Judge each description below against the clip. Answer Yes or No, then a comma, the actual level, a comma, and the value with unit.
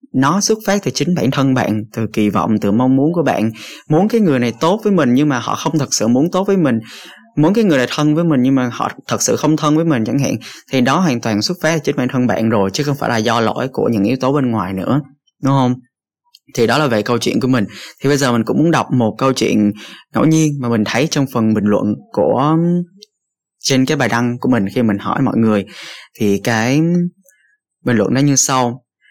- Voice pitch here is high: No, low, 135 Hz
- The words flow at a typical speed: No, fast, 255 wpm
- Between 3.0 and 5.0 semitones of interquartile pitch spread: No, wide, 5.6 semitones